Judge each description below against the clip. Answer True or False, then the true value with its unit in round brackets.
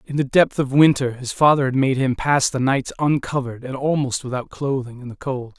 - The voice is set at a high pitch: False (135 Hz)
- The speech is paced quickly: True (225 wpm)